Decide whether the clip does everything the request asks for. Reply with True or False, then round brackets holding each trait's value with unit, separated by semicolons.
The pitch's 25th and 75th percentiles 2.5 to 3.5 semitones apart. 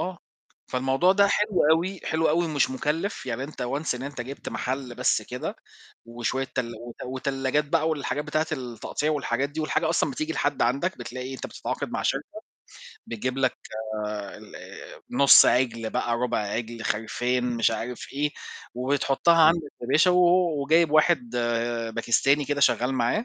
False (4.1 semitones)